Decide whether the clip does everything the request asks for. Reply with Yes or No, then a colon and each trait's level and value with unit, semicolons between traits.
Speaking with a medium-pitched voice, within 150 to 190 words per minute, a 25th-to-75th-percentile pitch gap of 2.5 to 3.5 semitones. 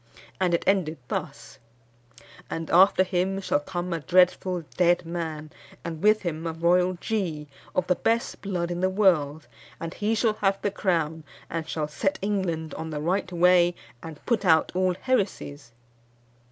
Yes: medium, 175 Hz; average, 165 wpm; average, 2.8 semitones